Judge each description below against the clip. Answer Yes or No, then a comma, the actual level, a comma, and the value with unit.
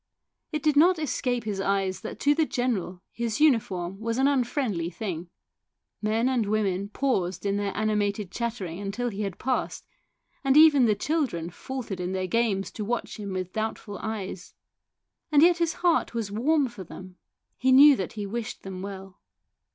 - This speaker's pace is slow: No, average, 175 wpm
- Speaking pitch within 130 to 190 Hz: No, high, 215 Hz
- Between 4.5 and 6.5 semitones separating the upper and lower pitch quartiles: Yes, average, 5.2 semitones